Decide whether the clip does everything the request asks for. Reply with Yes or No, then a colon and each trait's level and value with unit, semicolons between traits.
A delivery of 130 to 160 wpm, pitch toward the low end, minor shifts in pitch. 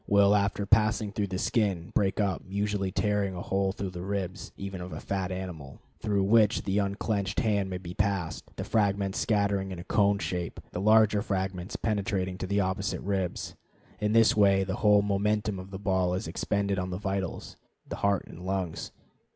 No: average, 190 wpm; low, 100 Hz; narrow, 1.6 semitones